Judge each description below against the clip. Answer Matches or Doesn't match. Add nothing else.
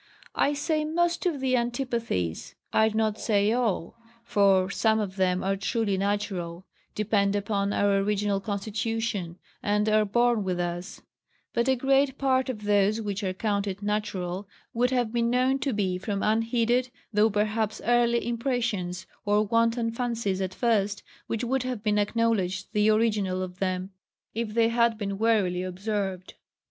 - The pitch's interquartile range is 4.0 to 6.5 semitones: Doesn't match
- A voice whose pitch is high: Matches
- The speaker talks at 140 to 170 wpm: Matches